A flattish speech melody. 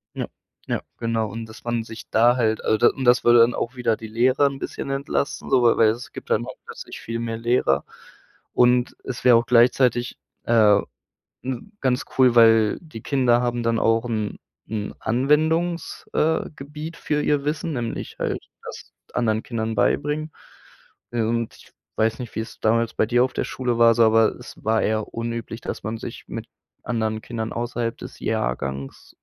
Yes: narrow, 2.2 semitones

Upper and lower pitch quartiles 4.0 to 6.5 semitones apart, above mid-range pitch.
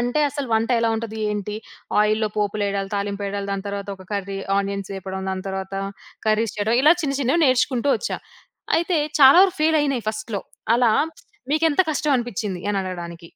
Yes: average, 5.0 semitones; high, 215 Hz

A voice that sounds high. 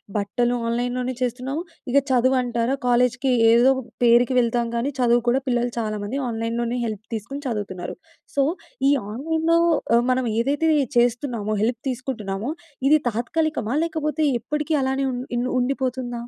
Yes: high, 245 Hz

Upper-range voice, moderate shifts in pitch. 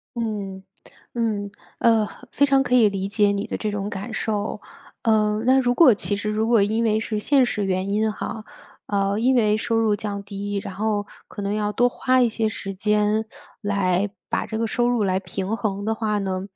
No: high, 210 Hz; narrow, 2.1 semitones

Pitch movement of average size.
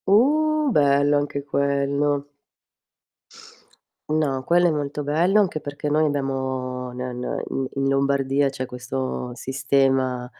No: narrow, 1.9 semitones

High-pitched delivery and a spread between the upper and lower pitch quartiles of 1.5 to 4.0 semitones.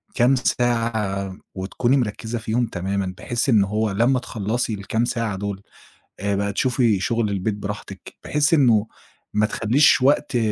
No: low, 110 Hz; average, 3.3 semitones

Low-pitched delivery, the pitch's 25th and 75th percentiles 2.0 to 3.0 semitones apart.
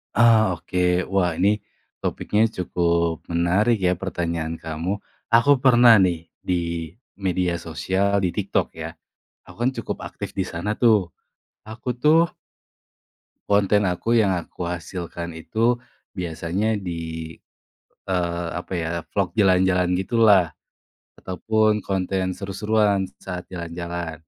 No: very low, 90 Hz; average, 3.4 semitones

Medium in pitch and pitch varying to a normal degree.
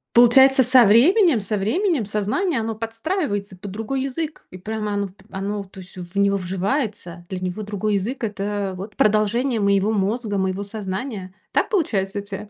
No: high, 210 Hz; average, 3.6 semitones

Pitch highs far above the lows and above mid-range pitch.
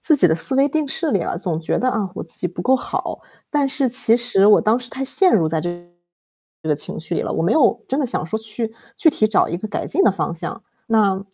Yes: wide, 6.8 semitones; high, 220 Hz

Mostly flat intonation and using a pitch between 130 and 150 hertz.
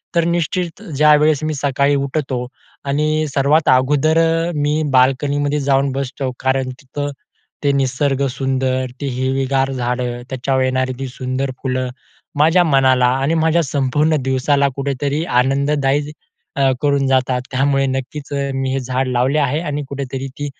Yes: narrow, 1.9 semitones; low, 135 Hz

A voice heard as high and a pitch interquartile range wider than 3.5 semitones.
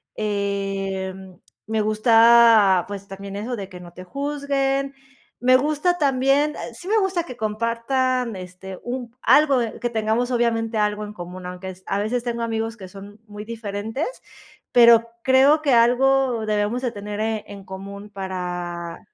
Yes: high, 220 Hz; average, 4.2 semitones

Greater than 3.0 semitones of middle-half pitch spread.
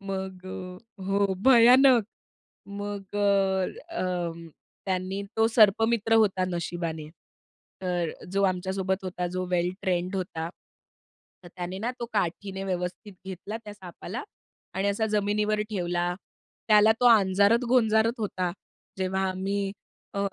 No: narrow, 2.4 semitones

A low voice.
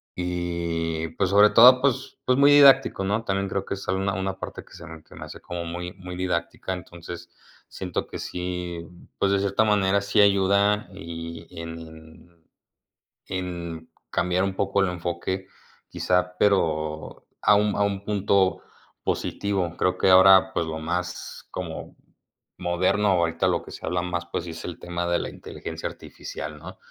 Yes: very low, 90 Hz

